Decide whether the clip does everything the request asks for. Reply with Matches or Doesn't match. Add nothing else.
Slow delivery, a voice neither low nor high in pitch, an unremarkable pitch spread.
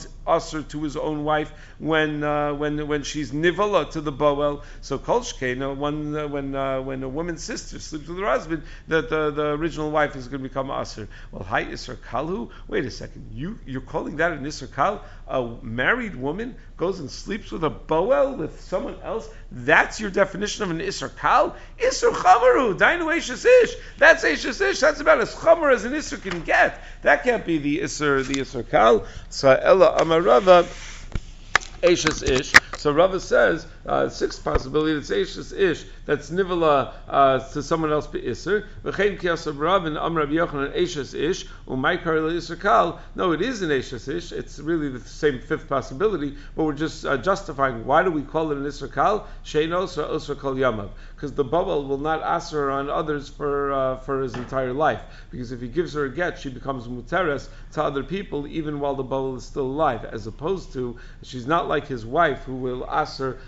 Doesn't match